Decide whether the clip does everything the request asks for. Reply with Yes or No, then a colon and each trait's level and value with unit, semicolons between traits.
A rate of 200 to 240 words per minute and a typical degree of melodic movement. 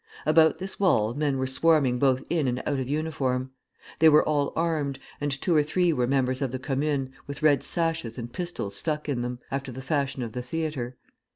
Yes: fast, 205 wpm; average, 3.3 semitones